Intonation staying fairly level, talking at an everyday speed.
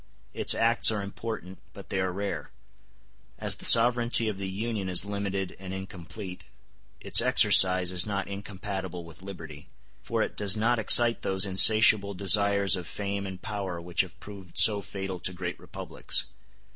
Yes: narrow, 2.0 semitones; average, 160 wpm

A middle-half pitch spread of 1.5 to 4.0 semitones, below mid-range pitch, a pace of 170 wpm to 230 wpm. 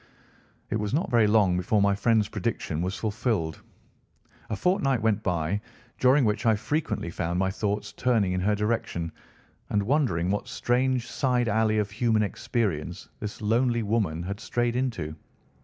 No: average, 3.6 semitones; low, 105 Hz; average, 155 wpm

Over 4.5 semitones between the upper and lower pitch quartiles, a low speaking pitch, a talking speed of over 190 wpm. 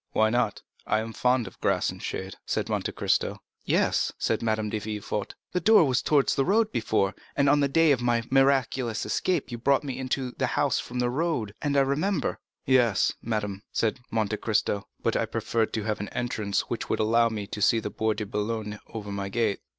No: average, 4.0 semitones; low, 115 Hz; fast, 205 wpm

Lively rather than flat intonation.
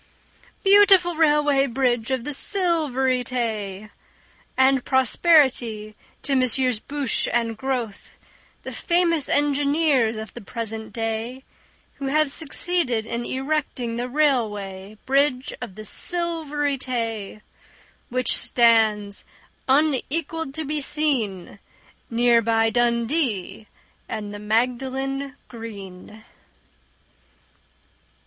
No: average, 4.5 semitones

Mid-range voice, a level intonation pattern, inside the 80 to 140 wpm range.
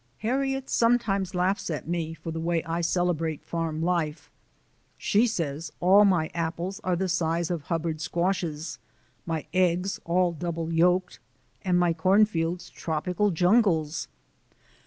Yes: medium, 175 Hz; narrow, 2.3 semitones; slow, 135 wpm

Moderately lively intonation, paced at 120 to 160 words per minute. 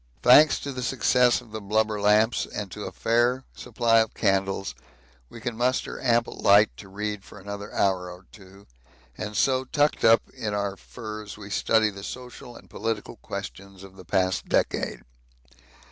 No: average, 3.2 semitones; average, 170 wpm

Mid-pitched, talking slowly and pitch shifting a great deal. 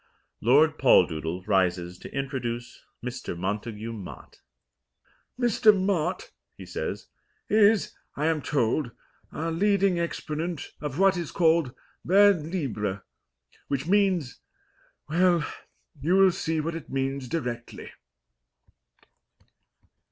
Yes: medium, 150 Hz; slow, 105 wpm; wide, 6.9 semitones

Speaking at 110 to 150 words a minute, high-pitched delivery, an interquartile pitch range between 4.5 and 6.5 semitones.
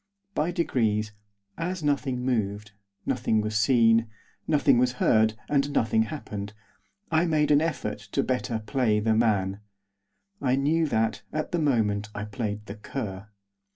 No: average, 145 wpm; low, 115 Hz; average, 5.1 semitones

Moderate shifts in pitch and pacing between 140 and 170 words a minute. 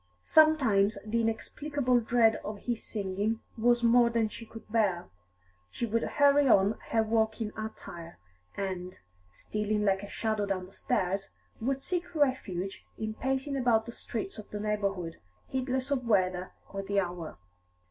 Yes: average, 3.6 semitones; average, 150 wpm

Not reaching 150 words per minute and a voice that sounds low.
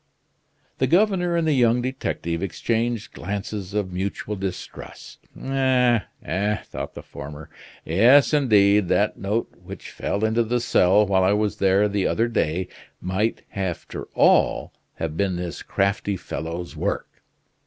Yes: average, 140 wpm; low, 105 Hz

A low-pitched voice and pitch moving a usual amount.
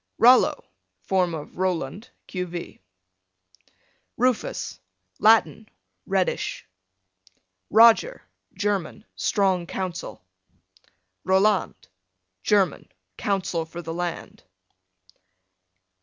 No: high, 190 Hz; average, 3.3 semitones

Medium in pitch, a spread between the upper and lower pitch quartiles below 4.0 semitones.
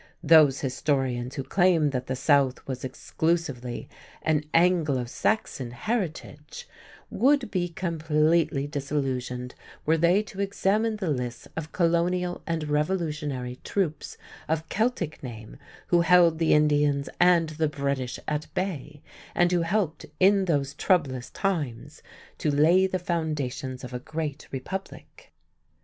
No: medium, 155 Hz; average, 4.3 semitones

